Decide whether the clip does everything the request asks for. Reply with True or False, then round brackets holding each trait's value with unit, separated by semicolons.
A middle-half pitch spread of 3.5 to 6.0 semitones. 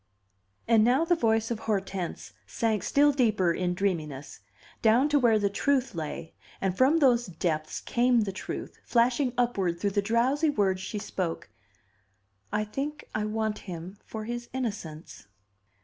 True (4.7 semitones)